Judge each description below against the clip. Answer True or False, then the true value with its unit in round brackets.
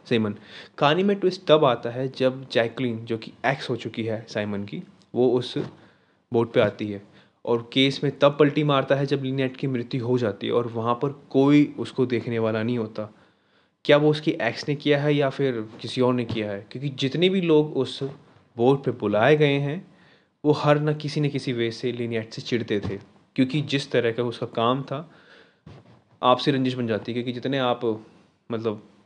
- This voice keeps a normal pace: False (200 wpm)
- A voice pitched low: True (125 Hz)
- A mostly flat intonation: False (3.6 semitones)